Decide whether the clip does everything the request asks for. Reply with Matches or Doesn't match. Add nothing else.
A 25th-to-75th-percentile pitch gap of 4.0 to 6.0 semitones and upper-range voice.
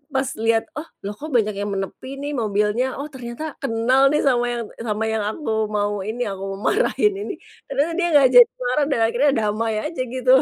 Matches